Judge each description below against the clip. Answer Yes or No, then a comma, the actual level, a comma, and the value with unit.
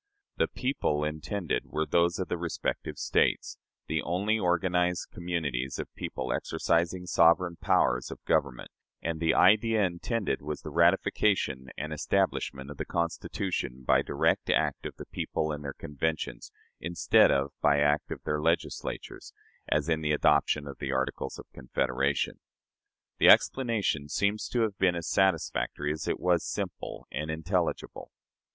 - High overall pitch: No, very low, 80 Hz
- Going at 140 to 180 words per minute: Yes, average, 150 wpm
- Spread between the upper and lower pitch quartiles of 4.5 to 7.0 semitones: No, average, 3.6 semitones